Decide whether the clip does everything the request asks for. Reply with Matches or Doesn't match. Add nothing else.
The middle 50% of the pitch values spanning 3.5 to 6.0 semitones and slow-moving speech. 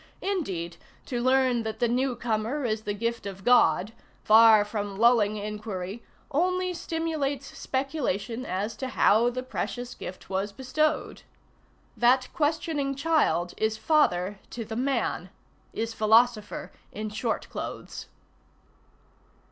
Matches